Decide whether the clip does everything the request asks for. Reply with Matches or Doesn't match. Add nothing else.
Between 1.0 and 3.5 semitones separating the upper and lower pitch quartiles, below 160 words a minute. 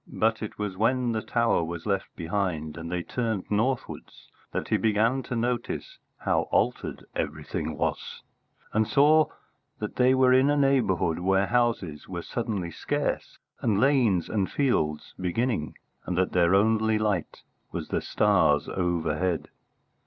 Doesn't match